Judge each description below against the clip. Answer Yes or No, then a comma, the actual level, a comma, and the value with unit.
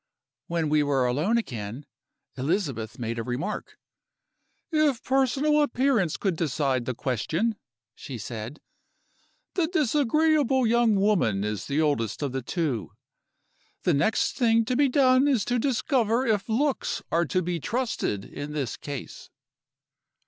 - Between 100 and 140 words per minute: Yes, slow, 135 wpm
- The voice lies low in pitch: No, medium, 185 Hz